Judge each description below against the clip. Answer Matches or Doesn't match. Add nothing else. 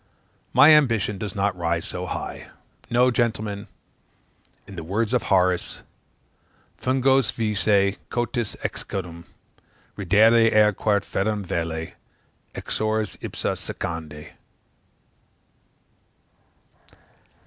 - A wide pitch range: Doesn't match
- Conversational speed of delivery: Doesn't match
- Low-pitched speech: Matches